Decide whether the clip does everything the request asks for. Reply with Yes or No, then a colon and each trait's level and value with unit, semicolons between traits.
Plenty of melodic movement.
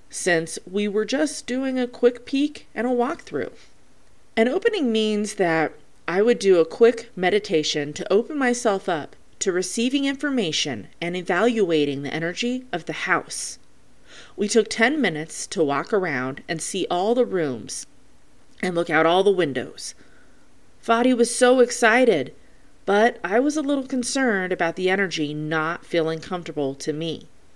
Yes: wide, 6.8 semitones